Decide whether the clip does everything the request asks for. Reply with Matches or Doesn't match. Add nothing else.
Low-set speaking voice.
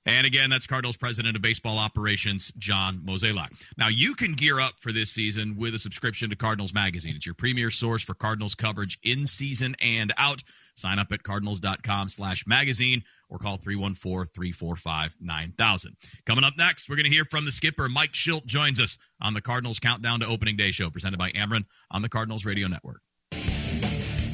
Matches